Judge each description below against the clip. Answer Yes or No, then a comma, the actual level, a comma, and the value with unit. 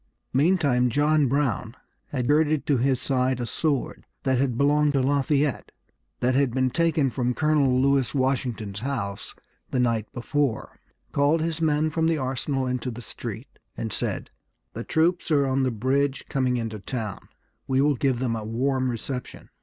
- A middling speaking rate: Yes, average, 165 wpm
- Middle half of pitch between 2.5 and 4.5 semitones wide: Yes, average, 2.8 semitones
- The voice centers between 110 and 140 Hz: Yes, low, 135 Hz